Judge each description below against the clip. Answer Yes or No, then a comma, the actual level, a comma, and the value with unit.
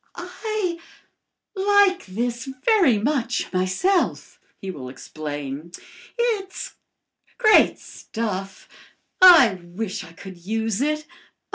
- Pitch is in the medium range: No, high, 230 Hz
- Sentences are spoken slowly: Yes, slow, 95 wpm